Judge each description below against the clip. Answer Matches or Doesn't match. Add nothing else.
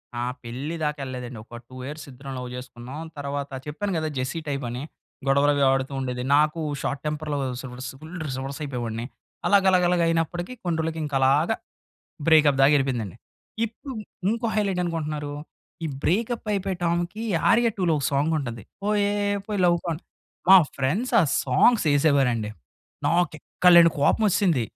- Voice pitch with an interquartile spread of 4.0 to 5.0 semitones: Matches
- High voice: Doesn't match